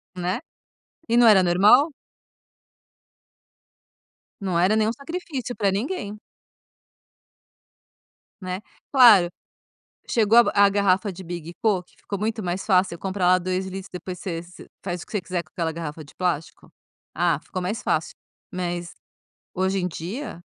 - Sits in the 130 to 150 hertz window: No, medium, 185 Hz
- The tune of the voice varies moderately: Yes, average, 3.1 semitones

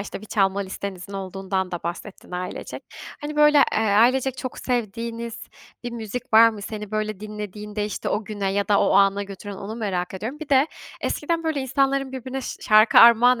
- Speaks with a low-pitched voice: No, high, 215 Hz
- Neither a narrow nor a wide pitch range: Yes, average, 4.0 semitones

